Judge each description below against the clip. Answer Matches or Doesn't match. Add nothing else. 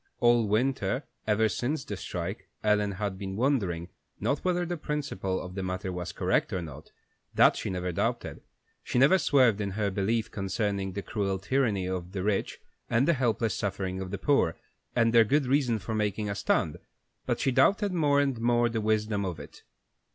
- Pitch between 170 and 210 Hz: Doesn't match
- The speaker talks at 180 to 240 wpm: Matches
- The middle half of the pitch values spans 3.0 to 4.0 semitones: Doesn't match